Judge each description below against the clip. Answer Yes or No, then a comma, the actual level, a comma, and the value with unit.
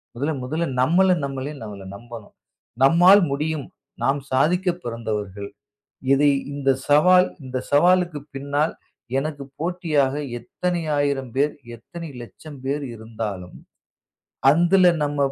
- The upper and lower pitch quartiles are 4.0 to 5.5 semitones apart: Yes, average, 4.5 semitones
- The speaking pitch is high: No, medium, 145 Hz